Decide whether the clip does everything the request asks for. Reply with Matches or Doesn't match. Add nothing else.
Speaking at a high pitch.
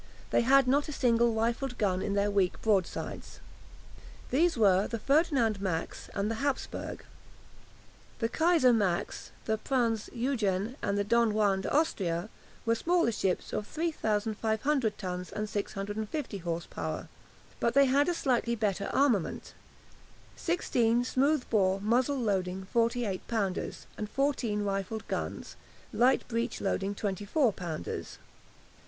Matches